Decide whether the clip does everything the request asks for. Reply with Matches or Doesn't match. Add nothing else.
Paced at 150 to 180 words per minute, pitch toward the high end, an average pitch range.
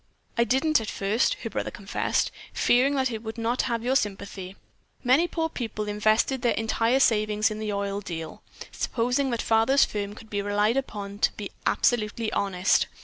Matches